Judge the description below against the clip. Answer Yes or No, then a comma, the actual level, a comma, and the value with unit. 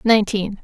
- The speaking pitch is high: Yes, high, 210 Hz